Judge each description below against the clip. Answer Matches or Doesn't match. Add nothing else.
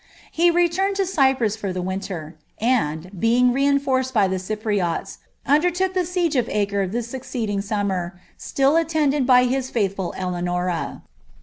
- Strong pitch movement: Matches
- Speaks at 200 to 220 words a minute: Doesn't match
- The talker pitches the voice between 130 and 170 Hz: Doesn't match